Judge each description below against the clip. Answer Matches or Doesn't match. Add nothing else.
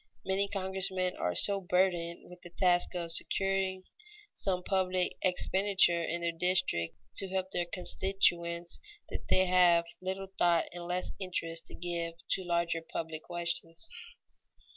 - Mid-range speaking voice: Matches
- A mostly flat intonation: Matches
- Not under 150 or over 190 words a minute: Doesn't match